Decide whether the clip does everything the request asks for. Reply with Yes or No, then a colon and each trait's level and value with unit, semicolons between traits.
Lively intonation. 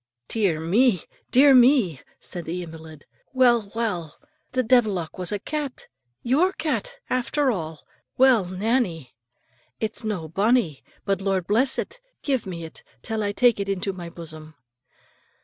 Yes: wide, 6.7 semitones